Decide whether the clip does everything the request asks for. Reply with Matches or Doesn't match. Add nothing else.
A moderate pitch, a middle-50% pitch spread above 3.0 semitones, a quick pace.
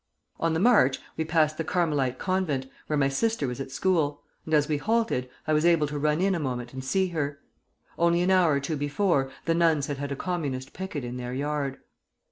Matches